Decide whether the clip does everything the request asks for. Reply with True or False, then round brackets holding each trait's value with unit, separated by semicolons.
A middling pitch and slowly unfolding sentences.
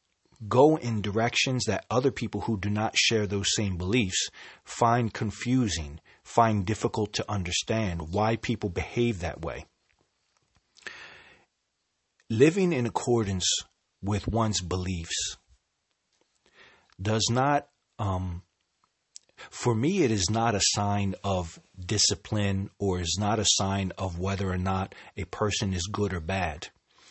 False (105 Hz; 125 wpm)